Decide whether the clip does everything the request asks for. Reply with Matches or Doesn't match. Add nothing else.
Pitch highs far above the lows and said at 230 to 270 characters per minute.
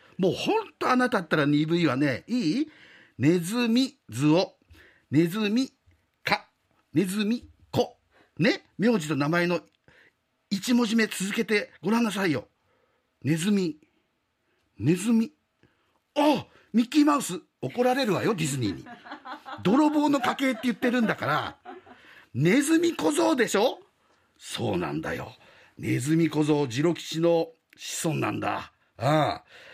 Matches